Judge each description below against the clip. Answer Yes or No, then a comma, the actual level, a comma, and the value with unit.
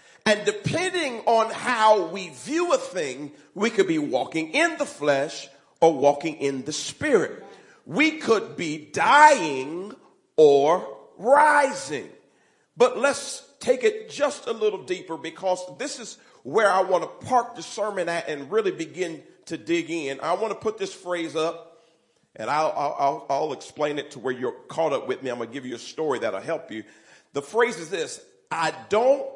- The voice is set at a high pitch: Yes, high, 225 Hz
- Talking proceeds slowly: No, average, 180 wpm